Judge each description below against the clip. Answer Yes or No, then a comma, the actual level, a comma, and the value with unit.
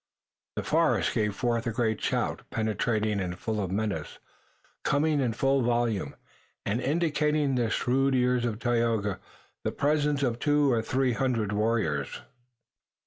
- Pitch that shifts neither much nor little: Yes, average, 3.8 semitones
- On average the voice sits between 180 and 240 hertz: No, low, 120 Hz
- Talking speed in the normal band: Yes, average, 145 wpm